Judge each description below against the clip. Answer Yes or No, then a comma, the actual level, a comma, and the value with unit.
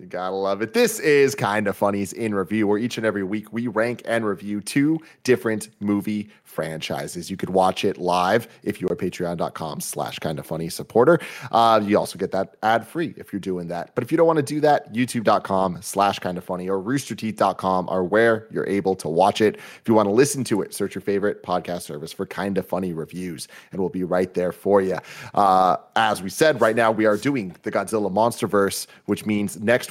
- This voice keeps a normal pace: No, fast, 215 wpm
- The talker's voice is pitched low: Yes, low, 100 Hz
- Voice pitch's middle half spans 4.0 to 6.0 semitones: No, average, 3.5 semitones